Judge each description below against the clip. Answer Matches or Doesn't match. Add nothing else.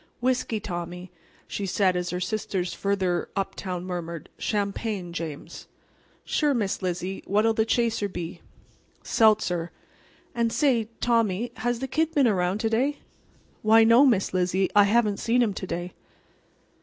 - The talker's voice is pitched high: Matches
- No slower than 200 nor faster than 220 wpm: Doesn't match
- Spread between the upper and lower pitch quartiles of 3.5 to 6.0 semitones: Matches